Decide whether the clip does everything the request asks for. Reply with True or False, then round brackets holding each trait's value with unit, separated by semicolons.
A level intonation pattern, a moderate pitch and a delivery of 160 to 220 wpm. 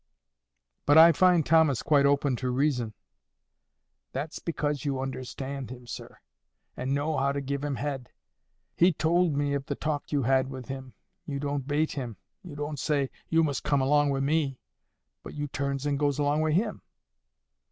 True (2.0 semitones; 145 Hz; 175 wpm)